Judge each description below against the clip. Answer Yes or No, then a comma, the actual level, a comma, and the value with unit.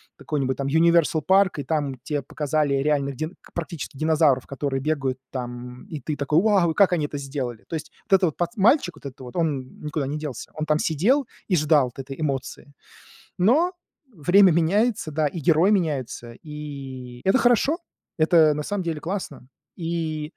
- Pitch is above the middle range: No, medium, 155 Hz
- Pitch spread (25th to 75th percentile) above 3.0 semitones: Yes, average, 3.8 semitones